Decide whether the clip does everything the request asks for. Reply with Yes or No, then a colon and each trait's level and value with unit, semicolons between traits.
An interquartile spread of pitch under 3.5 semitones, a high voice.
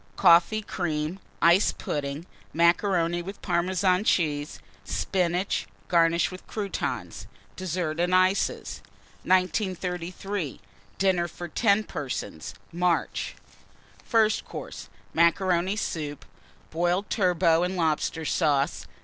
No: narrow, 2.4 semitones; medium, 175 Hz